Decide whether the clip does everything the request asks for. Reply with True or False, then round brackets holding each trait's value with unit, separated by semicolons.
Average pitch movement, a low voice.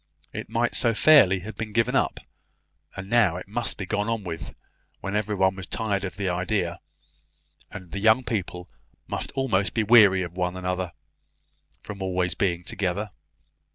True (3.0 semitones; 95 Hz)